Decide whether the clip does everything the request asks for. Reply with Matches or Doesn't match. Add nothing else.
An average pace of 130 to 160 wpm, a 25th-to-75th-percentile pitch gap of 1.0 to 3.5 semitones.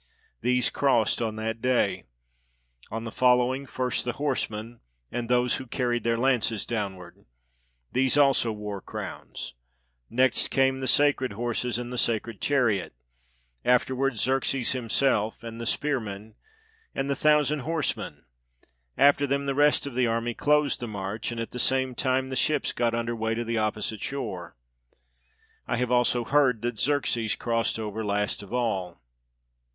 Matches